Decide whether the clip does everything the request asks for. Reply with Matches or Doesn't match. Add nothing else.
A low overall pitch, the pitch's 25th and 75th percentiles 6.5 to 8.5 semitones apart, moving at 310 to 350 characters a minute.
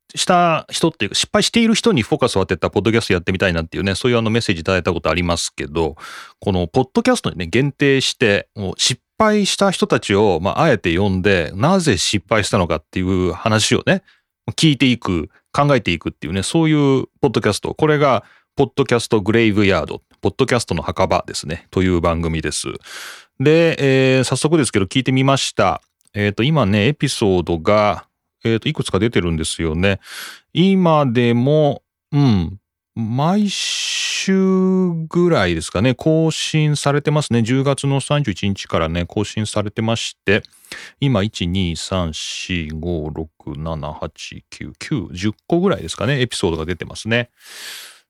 Matches